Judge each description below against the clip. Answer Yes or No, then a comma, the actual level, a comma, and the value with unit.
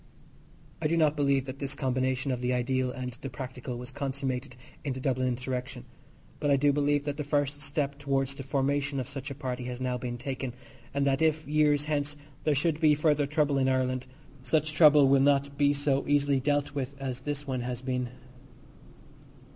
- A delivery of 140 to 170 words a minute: No, average, 195 wpm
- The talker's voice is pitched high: No, medium, 140 Hz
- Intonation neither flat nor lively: No, narrow, 2.0 semitones